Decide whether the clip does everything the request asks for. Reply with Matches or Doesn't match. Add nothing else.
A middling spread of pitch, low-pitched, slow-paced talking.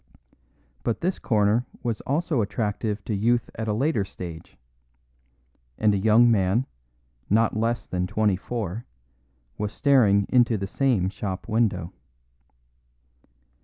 Matches